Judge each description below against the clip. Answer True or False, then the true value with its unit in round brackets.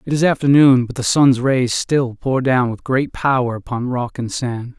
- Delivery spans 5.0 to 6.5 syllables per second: False (4.5 syllables/s)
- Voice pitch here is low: True (130 Hz)